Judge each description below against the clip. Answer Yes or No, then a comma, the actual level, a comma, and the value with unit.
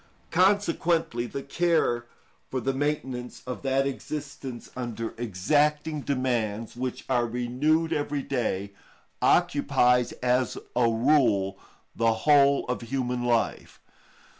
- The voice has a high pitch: No, low, 125 Hz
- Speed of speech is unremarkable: No, slow, 110 wpm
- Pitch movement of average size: Yes, average, 3.4 semitones